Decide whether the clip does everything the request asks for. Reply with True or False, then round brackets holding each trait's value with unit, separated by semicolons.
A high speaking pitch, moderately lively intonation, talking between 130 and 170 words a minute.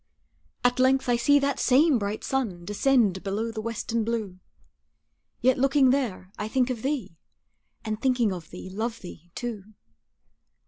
True (230 Hz; 4.2 semitones; 150 wpm)